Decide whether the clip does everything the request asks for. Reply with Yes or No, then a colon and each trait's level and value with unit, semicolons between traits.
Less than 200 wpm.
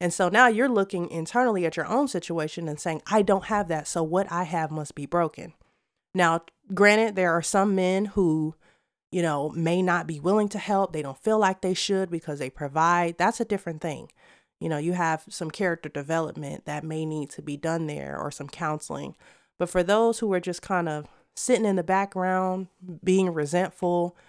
No: fast, 205 wpm